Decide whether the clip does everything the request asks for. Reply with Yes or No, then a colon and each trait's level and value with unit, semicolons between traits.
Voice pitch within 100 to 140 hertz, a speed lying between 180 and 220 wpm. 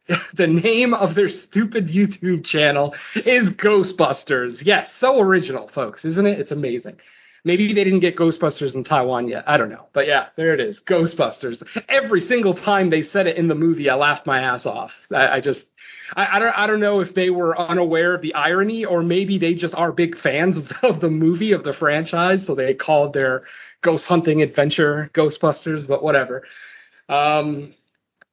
No: medium, 170 Hz; average, 185 wpm